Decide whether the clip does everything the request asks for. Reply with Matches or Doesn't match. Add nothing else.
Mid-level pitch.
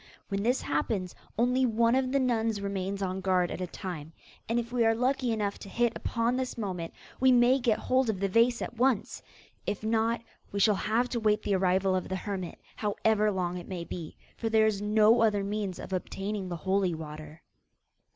Doesn't match